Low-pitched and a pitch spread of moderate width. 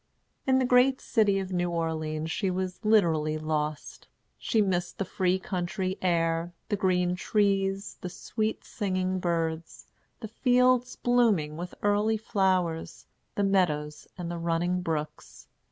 No: medium, 185 Hz; average, 3.7 semitones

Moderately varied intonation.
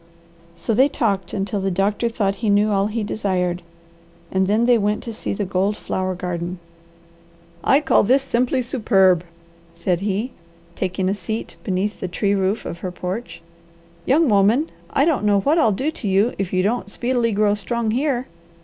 Yes: average, 3.8 semitones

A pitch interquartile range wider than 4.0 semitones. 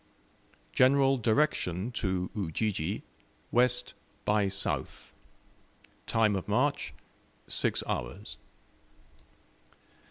Yes: average, 4.5 semitones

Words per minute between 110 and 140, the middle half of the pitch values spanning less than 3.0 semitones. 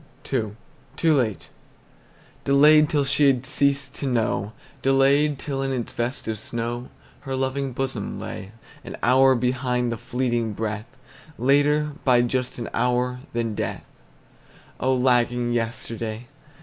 Yes: slow, 135 wpm; narrow, 2.4 semitones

